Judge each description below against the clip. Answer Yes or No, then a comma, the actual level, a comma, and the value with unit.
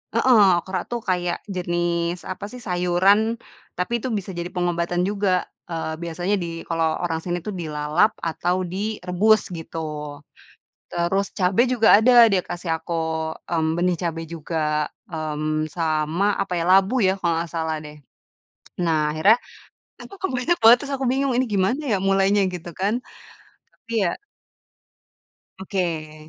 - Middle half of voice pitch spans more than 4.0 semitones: No, average, 3.5 semitones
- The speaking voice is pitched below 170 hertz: No, medium, 180 Hz